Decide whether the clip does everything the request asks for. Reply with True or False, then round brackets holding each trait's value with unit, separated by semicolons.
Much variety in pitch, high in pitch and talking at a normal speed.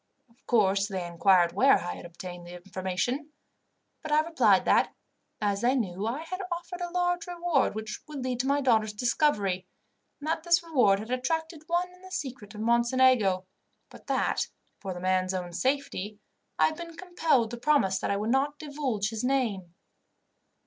True (7.6 semitones; 245 Hz; 180 wpm)